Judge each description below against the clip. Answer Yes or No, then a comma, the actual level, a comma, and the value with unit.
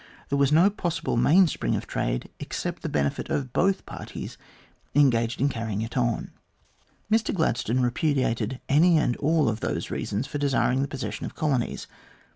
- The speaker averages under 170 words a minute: Yes, average, 160 wpm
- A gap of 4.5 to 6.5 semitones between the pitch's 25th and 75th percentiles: Yes, average, 5.0 semitones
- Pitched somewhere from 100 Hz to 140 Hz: Yes, low, 135 Hz